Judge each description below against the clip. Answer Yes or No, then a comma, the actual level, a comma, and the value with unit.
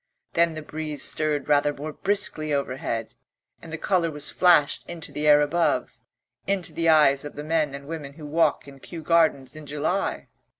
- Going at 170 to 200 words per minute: Yes, average, 180 wpm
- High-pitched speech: No, medium, 155 Hz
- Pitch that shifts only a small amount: Yes, narrow, 2.2 semitones